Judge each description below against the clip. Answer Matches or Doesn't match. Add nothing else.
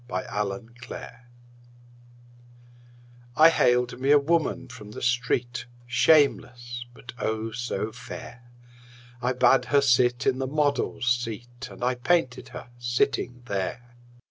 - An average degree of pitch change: Doesn't match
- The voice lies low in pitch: Matches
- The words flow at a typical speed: Doesn't match